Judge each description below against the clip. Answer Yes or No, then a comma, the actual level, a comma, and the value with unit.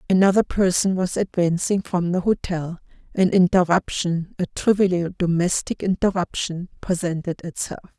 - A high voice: No, medium, 180 Hz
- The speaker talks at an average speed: No, slow, 115 wpm